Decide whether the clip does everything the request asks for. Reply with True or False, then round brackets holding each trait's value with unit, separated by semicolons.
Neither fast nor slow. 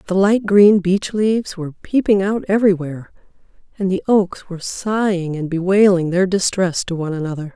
True (165 wpm)